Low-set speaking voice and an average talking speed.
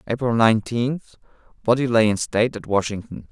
Yes: low, 115 Hz; average, 145 wpm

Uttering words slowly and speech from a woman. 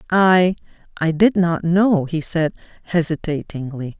Yes: slow, 105 wpm; female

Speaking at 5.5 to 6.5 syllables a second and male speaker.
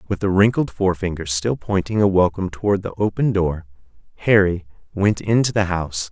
Yes: 5.7 syllables/s; male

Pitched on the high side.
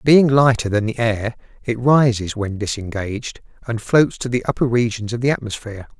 No: low, 115 Hz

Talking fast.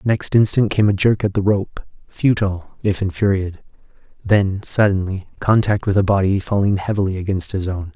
No: average, 165 wpm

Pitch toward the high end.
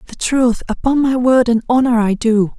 Yes: high, 240 Hz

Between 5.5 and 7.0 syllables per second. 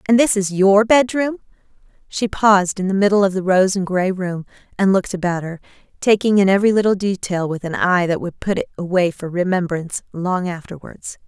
Yes: 5.6 syllables/s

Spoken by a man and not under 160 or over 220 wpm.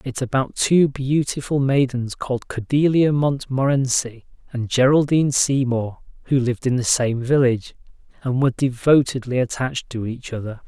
No: male; slow, 135 wpm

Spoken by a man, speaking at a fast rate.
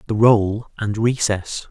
No: male; average, 140 wpm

